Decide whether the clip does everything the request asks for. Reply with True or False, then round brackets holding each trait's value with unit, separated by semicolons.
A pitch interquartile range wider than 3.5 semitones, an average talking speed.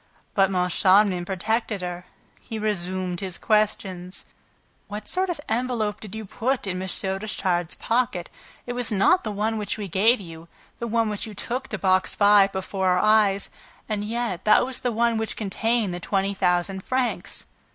False (3.0 semitones; 170 wpm)